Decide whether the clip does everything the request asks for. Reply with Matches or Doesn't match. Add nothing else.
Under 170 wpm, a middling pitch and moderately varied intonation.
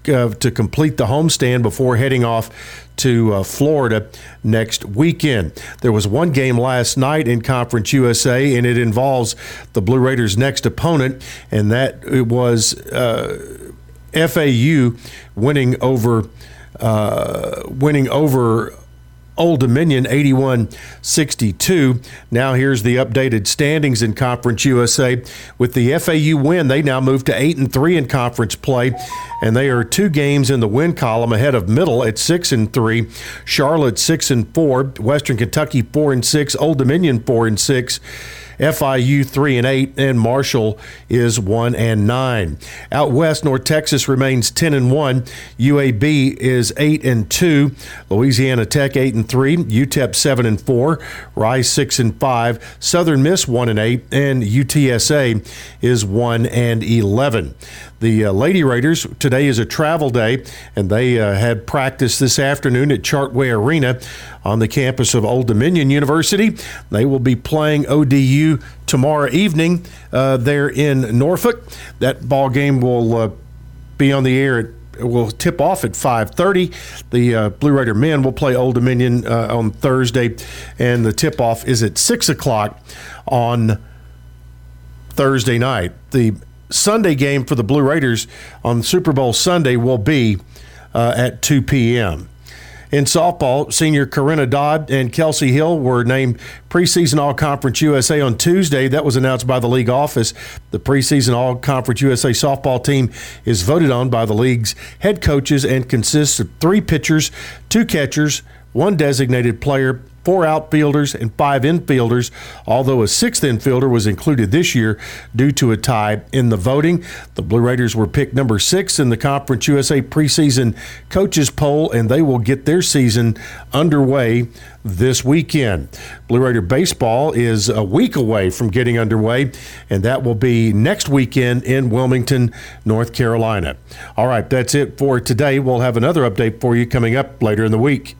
Doesn't match